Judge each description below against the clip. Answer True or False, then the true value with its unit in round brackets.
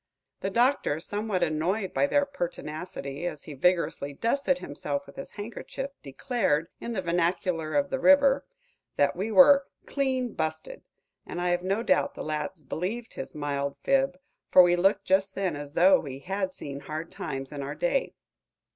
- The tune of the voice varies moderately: False (8.3 semitones)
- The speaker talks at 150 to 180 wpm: True (170 wpm)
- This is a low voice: False (185 Hz)